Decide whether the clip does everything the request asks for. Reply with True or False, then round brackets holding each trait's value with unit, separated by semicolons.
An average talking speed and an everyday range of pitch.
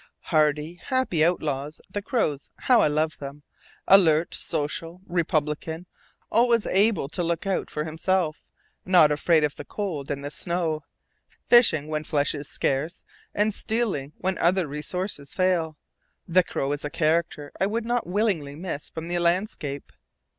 True (150 wpm; 3.9 semitones)